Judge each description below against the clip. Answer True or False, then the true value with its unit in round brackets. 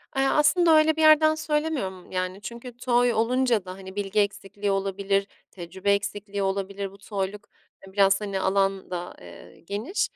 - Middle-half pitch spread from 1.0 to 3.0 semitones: False (4.2 semitones)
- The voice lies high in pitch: True (200 Hz)